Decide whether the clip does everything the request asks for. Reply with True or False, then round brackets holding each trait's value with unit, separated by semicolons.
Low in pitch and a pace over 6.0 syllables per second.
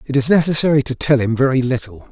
True (130 Hz; 6.5 syllables/s)